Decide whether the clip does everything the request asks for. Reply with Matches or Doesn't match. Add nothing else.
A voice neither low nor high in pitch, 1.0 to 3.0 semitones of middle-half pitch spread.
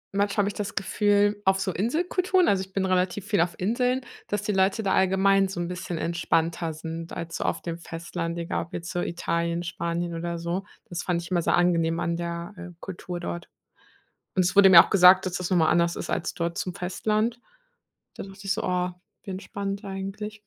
Matches